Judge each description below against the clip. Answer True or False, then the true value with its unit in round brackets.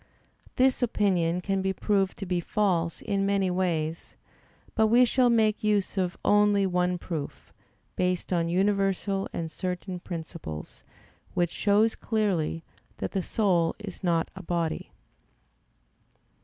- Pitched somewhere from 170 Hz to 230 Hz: True (190 Hz)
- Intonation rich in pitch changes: False (3.0 semitones)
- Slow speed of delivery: True (130 wpm)